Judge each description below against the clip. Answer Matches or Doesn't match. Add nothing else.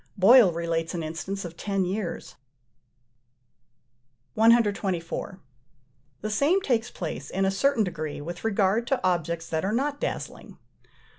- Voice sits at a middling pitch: Doesn't match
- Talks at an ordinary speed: Doesn't match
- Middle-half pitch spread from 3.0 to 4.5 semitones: Doesn't match